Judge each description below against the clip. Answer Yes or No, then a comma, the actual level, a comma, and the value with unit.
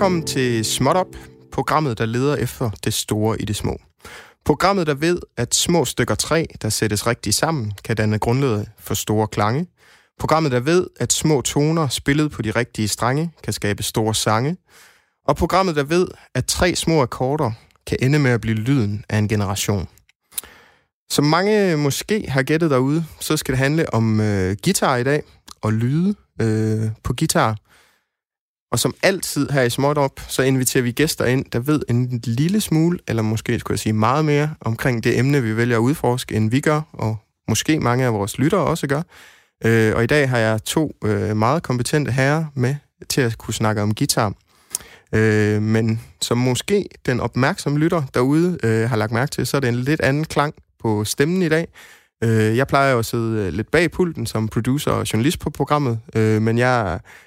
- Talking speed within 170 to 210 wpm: Yes, average, 190 wpm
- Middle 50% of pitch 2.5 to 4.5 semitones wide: No, wide, 5.4 semitones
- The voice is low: Yes, low, 125 Hz